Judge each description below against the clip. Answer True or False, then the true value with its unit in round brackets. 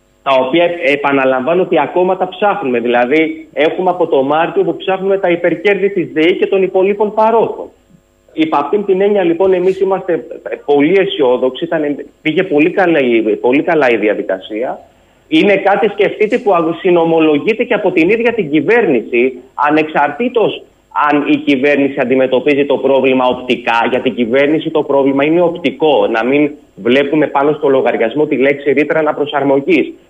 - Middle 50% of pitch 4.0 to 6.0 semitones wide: True (5.5 semitones)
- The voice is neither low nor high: True (155 Hz)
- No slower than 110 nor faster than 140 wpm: False (150 wpm)